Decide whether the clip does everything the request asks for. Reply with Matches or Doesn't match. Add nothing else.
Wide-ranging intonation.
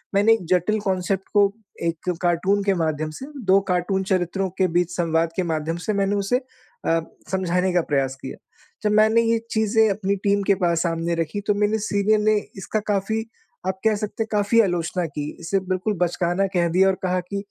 Doesn't match